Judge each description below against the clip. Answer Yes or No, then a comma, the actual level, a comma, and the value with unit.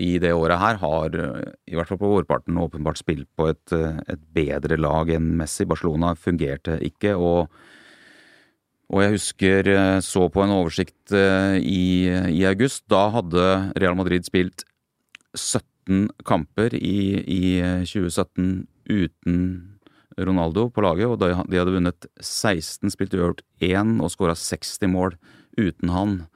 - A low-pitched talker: Yes, very low, 90 Hz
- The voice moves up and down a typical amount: No, narrow, 2.2 semitones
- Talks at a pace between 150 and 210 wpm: No, average, 140 wpm